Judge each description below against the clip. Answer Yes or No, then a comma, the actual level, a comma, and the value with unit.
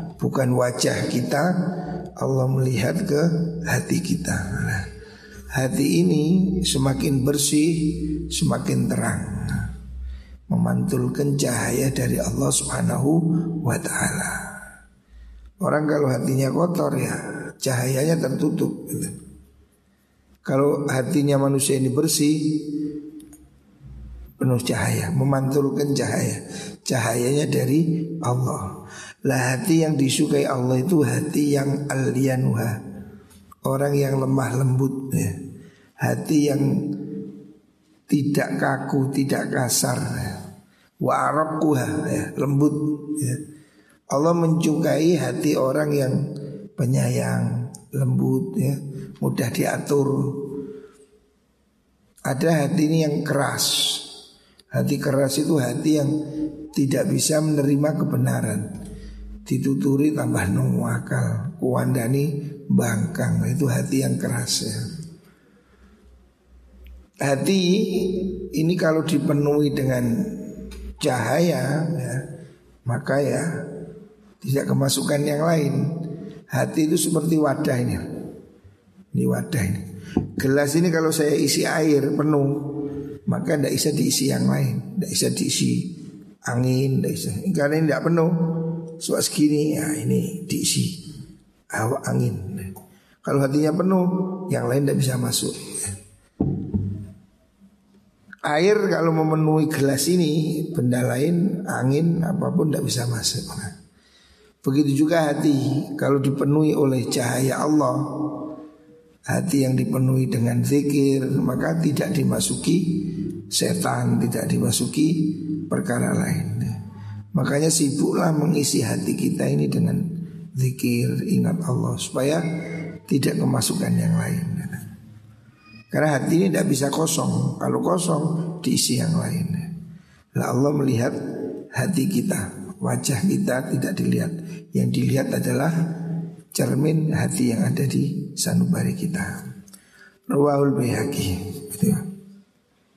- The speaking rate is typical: Yes, average, 100 wpm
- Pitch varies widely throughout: No, average, 4.4 semitones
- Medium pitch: Yes, medium, 145 Hz